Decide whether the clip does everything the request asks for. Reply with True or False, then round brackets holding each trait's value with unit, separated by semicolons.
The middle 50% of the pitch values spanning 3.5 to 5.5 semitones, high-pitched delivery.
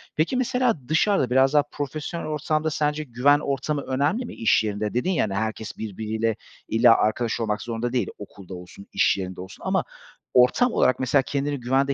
False (5.2 semitones; 130 Hz)